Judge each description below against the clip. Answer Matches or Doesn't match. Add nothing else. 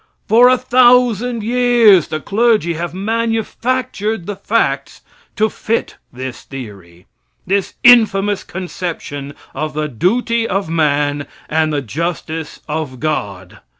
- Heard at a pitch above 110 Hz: Matches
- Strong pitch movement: Matches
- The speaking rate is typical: Doesn't match